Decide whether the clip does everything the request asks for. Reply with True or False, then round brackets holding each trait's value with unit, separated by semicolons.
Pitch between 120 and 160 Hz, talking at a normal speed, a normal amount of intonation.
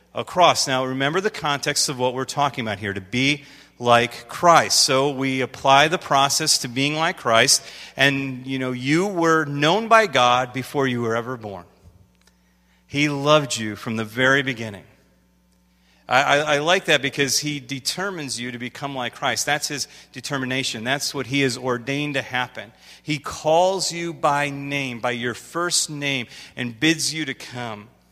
True (135 Hz; 175 wpm; 3.3 semitones)